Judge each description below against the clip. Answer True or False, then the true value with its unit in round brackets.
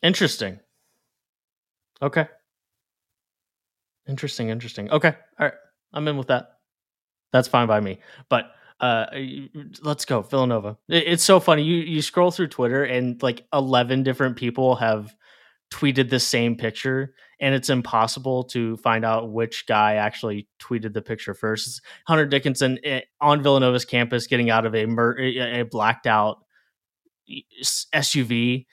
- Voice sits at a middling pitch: False (125 Hz)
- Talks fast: False (135 wpm)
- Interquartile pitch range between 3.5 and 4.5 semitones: True (4.0 semitones)